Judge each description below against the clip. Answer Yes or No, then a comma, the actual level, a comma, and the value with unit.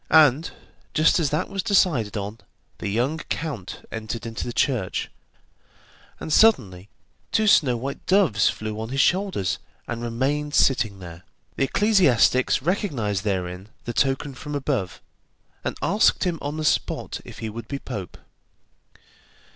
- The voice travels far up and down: Yes, wide, 6.4 semitones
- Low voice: Yes, low, 130 Hz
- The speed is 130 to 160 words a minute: Yes, average, 145 wpm